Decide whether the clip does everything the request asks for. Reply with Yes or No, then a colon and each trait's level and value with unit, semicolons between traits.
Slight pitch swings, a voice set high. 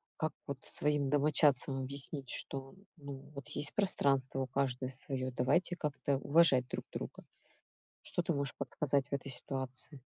No: narrow, 1.8 semitones; medium, 140 Hz